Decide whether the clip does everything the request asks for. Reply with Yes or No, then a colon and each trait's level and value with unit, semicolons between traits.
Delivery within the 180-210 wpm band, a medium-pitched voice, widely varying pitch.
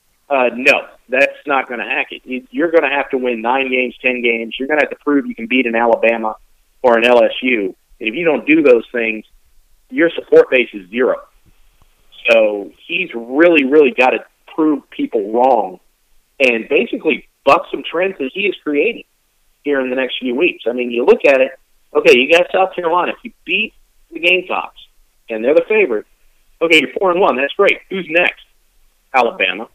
Yes: average, 200 wpm; medium, 145 Hz; wide, 8.3 semitones